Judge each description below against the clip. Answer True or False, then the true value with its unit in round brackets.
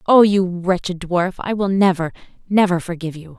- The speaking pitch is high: False (180 Hz)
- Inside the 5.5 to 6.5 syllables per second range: False (5.3 syllables/s)